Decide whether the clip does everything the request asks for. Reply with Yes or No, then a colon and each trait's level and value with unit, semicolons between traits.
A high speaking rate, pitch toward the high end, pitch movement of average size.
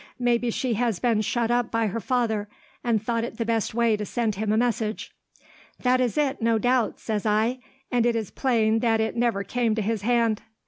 No: fast, 215 wpm; high, 230 Hz; narrow, 1.8 semitones